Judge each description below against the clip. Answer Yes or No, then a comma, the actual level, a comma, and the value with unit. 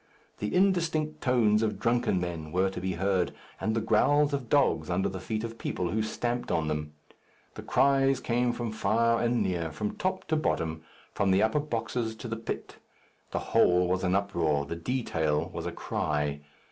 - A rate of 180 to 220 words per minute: Yes, average, 185 wpm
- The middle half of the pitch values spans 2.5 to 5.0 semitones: No, wide, 5.5 semitones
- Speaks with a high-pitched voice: No, low, 110 Hz